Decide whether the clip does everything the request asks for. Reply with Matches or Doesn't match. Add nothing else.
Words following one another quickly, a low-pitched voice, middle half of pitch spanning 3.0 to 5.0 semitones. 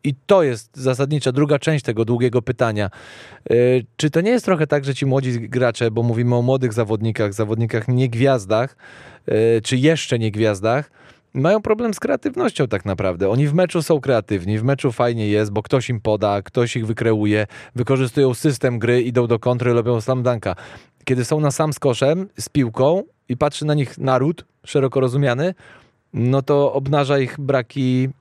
Matches